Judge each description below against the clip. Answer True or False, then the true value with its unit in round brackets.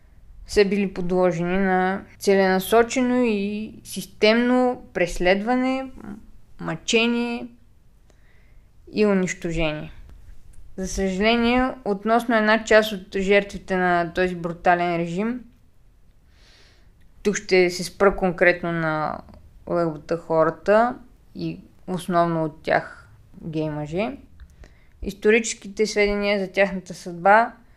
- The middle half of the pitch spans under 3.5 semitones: False (4.0 semitones)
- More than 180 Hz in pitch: True (190 Hz)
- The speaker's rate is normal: False (85 wpm)